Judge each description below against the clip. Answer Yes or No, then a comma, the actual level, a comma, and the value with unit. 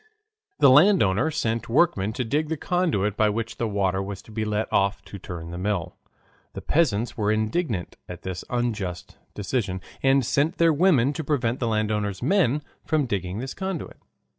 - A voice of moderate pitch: No, low, 115 Hz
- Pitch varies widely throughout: Yes, wide, 6.4 semitones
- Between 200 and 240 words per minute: No, average, 175 wpm